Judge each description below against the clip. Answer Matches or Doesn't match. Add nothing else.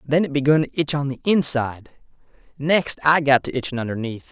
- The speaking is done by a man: Matches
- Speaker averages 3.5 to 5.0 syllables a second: Doesn't match